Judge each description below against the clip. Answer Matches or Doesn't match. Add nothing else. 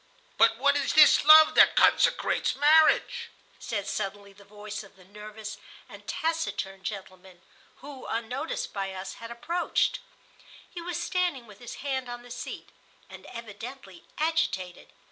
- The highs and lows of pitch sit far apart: Matches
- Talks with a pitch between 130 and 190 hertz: Doesn't match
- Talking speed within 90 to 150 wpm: Matches